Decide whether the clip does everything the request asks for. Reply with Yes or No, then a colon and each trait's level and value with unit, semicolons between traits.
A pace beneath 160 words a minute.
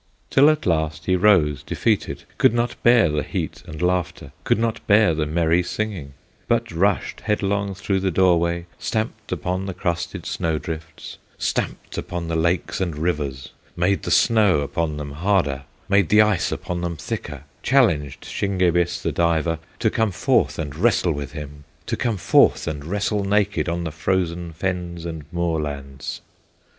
No: average, 165 wpm